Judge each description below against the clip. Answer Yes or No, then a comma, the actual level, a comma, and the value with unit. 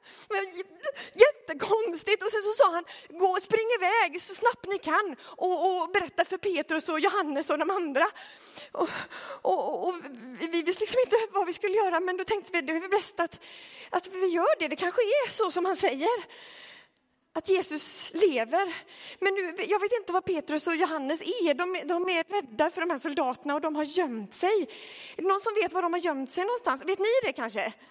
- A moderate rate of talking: No, fast, 205 wpm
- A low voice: No, very high, 365 Hz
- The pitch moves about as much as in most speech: Yes, average, 3.7 semitones